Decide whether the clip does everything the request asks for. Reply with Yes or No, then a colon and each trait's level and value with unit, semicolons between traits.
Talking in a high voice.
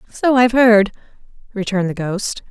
Yes: high, 215 Hz